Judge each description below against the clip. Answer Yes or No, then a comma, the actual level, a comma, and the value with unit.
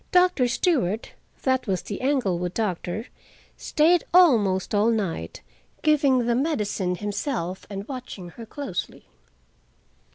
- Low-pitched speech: No, high, 225 Hz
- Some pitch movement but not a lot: No, wide, 6.4 semitones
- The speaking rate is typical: No, slow, 100 wpm